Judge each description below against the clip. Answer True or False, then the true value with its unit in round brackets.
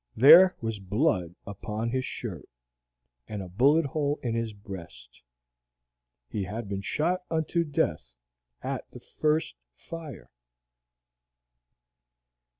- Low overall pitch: True (115 Hz)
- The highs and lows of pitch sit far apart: True (7.6 semitones)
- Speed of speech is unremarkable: False (110 wpm)